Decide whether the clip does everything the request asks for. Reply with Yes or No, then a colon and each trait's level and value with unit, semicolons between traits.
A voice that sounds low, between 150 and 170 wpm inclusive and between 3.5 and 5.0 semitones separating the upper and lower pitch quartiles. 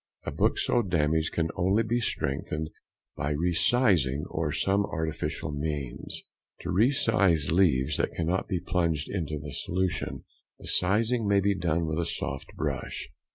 Yes: very low, 85 Hz; average, 155 wpm; average, 4.4 semitones